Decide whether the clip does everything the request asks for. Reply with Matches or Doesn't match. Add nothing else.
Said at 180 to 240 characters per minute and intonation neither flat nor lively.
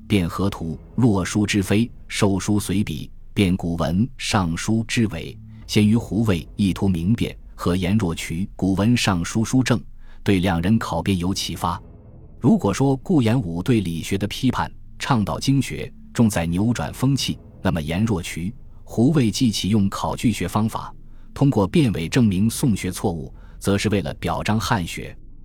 Matches